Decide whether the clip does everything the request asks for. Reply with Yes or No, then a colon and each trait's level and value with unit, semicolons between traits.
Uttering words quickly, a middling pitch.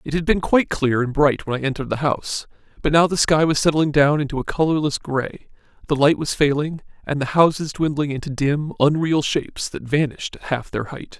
Yes: fast, 220 wpm; medium, 145 Hz